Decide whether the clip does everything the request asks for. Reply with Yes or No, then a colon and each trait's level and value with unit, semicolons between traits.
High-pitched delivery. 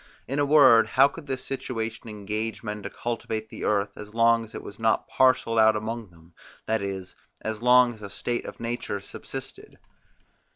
No: low, 115 Hz